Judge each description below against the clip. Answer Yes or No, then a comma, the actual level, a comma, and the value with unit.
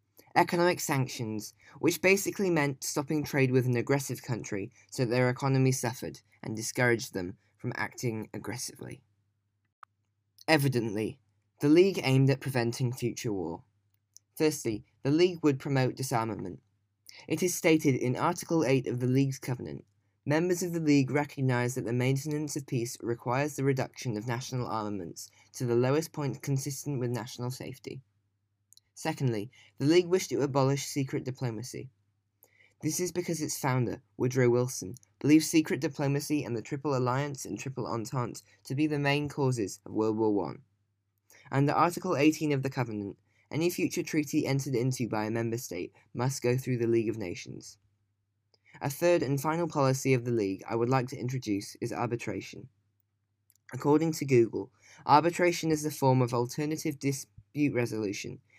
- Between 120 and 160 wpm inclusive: Yes, average, 155 wpm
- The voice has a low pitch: Yes, low, 125 Hz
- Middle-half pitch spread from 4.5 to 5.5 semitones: Yes, average, 5.1 semitones